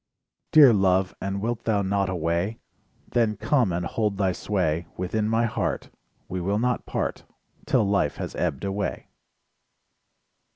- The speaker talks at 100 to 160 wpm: Yes, average, 140 wpm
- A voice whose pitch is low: Yes, low, 100 Hz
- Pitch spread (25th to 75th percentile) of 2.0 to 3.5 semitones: Yes, average, 3.1 semitones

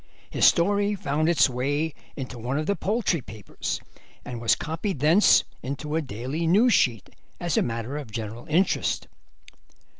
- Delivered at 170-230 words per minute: No, average, 155 wpm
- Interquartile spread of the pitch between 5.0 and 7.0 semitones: Yes, wide, 5.6 semitones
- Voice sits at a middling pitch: Yes, medium, 150 Hz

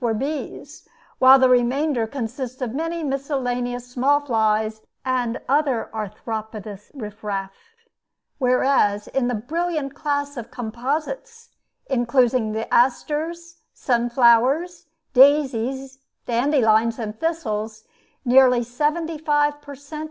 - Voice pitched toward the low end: No, very high, 255 Hz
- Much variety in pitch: No, average, 4.2 semitones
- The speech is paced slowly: Yes, slow, 105 wpm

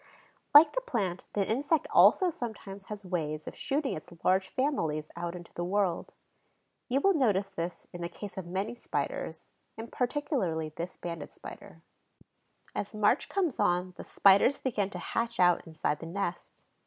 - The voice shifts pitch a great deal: Yes, wide, 5.9 semitones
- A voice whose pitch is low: No, high, 195 Hz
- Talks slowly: No, average, 165 wpm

